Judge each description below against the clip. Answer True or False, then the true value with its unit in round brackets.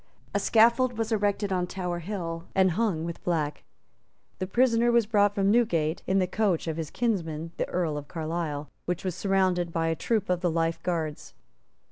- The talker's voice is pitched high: False (180 Hz)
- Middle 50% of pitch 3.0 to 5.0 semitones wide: True (3.9 semitones)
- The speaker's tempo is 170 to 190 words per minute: True (185 wpm)